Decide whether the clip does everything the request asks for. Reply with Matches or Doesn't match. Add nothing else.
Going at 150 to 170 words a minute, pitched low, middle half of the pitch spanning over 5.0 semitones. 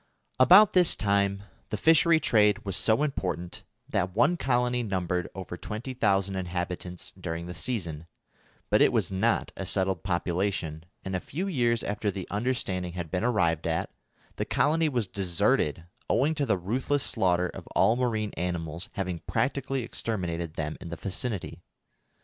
Matches